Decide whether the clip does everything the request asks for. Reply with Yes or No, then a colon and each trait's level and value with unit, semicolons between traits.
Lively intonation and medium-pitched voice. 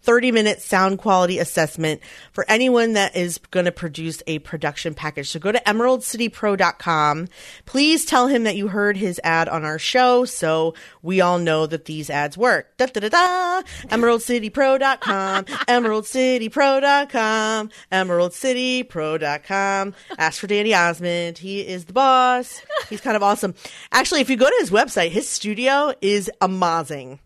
No: wide, 6.6 semitones; high, 205 Hz